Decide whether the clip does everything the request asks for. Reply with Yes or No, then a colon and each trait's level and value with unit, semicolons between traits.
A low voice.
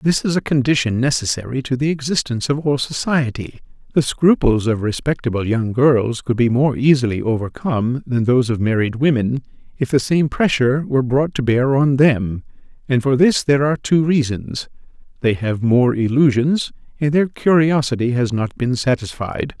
Yes: low, 130 Hz